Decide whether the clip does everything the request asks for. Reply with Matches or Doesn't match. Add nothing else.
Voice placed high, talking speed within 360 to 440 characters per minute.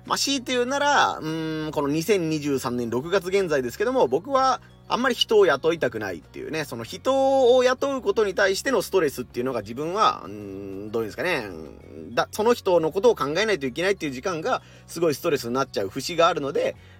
Matches